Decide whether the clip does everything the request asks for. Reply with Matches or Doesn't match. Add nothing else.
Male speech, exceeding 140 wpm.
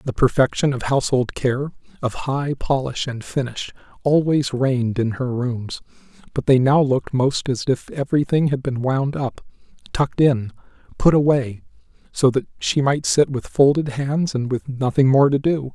Matches